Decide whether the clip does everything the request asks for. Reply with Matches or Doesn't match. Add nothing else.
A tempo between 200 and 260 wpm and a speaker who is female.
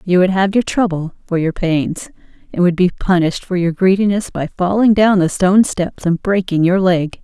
Matches